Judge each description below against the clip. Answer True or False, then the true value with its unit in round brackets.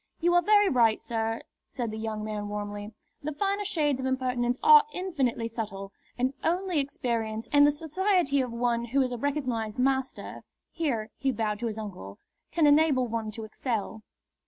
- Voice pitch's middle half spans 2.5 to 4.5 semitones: False (4.9 semitones)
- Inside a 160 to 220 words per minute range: True (175 wpm)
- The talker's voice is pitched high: True (250 Hz)